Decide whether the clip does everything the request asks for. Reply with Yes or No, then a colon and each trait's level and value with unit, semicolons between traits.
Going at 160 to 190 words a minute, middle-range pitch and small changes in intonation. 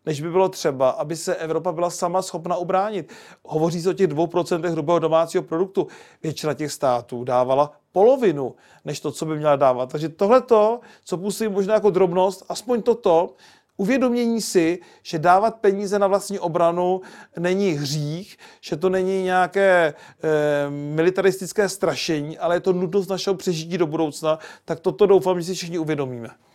No: average, 165 wpm; medium, 180 Hz; average, 3.4 semitones